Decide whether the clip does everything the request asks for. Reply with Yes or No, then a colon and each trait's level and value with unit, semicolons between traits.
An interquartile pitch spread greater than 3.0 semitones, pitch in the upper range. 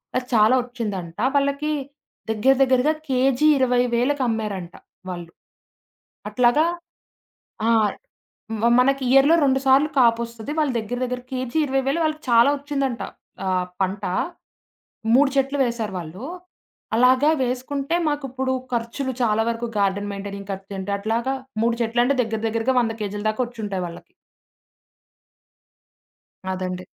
Yes: average, 4.1 semitones; high, 240 Hz